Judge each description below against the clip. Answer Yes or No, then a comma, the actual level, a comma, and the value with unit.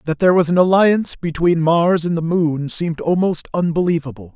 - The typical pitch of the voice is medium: Yes, medium, 170 Hz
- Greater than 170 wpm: Yes, average, 180 wpm